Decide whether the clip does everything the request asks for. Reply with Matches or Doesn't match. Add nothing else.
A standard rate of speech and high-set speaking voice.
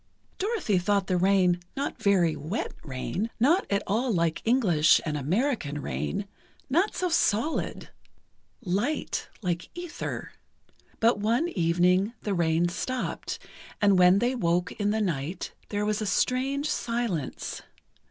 Doesn't match